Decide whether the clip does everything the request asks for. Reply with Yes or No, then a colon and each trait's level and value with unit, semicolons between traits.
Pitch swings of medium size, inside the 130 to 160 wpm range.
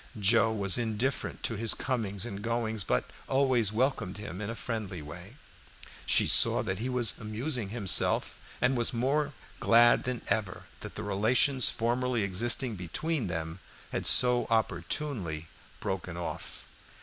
Yes: average, 4.1 semitones; average, 150 wpm